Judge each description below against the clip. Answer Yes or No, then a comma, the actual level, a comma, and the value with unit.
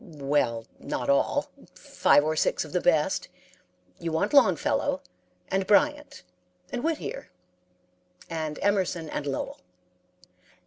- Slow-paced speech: Yes, slow, 115 wpm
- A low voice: No, medium, 160 Hz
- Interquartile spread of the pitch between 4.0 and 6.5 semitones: Yes, wide, 5.4 semitones